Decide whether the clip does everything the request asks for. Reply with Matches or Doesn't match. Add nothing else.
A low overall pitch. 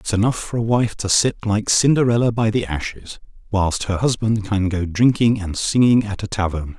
Matches